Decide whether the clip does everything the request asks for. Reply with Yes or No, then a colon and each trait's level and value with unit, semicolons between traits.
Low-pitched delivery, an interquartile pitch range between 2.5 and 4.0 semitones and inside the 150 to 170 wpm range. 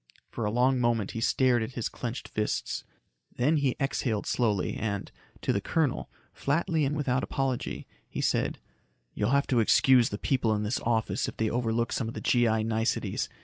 No: low, 120 Hz; average, 3.0 semitones; average, 185 wpm